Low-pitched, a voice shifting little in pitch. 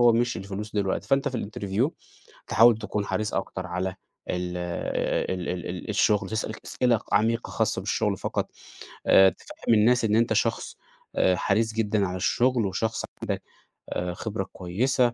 No: low, 105 Hz; average, 3.5 semitones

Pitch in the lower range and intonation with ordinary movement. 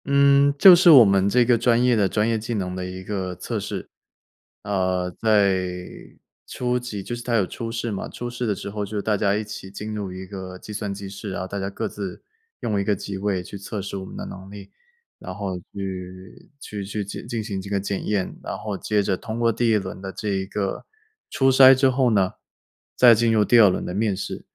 Yes: low, 105 Hz; average, 3.0 semitones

